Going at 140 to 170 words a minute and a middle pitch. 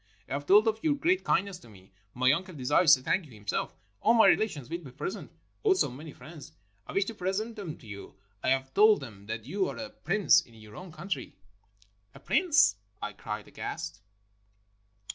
No: average, 200 wpm; medium, 165 Hz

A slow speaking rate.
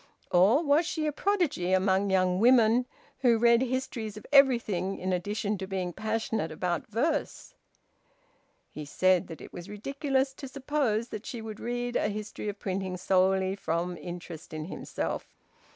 No: average, 155 wpm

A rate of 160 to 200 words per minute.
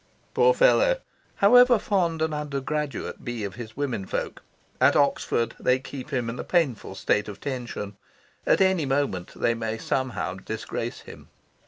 No: average, 150 wpm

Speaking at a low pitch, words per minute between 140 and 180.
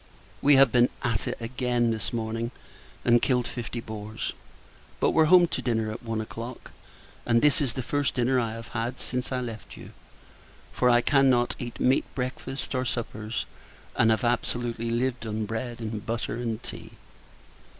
Yes: low, 120 Hz; average, 170 wpm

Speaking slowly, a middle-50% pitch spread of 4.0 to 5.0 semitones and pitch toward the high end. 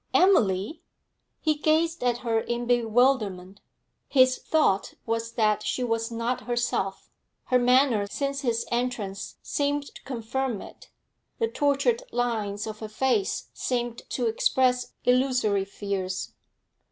No: slow, 125 wpm; average, 3.5 semitones; high, 240 Hz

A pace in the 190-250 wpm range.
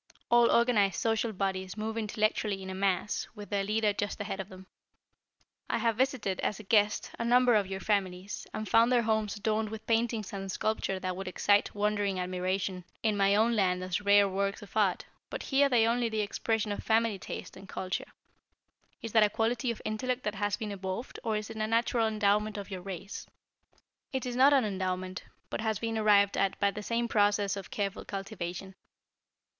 Yes: average, 200 wpm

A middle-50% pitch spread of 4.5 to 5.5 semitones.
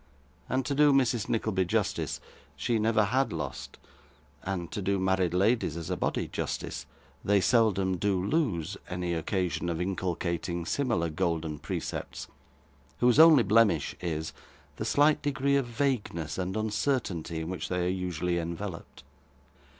Yes: average, 5.2 semitones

